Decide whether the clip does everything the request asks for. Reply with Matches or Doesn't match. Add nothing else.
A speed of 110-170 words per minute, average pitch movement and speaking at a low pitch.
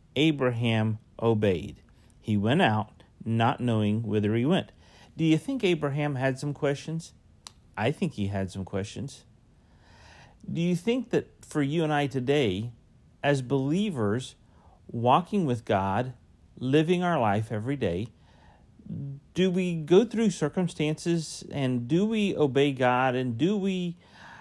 Doesn't match